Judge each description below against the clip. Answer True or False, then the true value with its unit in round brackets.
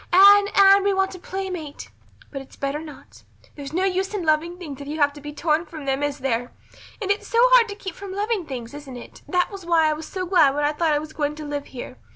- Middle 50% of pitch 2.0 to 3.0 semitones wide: False (4.8 semitones)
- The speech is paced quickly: True (265 wpm)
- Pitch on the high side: True (315 Hz)